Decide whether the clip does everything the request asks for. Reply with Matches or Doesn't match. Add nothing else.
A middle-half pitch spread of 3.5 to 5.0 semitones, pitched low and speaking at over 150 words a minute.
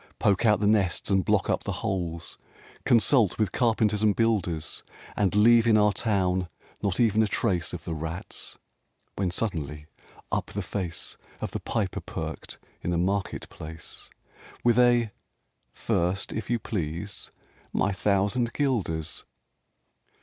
Doesn't match